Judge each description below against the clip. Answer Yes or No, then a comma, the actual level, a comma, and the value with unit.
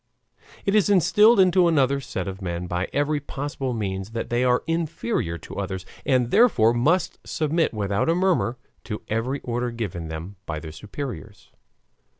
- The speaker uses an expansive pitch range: Yes, wide, 8.5 semitones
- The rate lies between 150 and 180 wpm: Yes, average, 160 wpm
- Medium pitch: No, low, 120 Hz